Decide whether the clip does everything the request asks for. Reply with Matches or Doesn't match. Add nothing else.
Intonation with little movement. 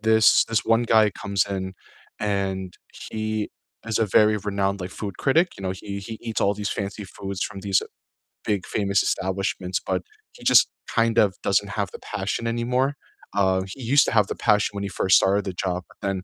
Matches